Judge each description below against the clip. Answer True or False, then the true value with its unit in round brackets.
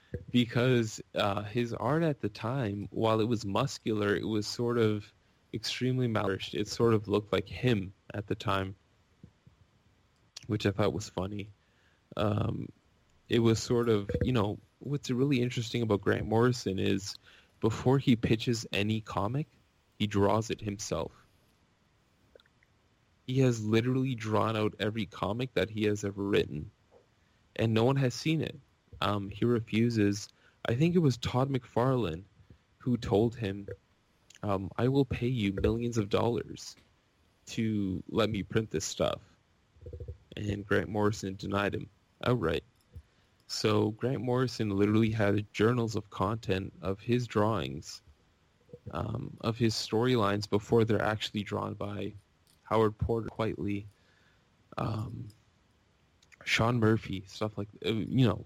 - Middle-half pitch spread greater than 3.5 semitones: False (2.9 semitones)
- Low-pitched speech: True (105 Hz)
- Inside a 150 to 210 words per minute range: False (140 wpm)